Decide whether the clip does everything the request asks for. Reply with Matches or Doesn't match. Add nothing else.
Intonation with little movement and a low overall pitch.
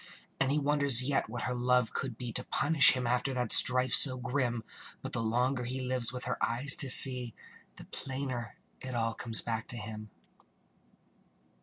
Matches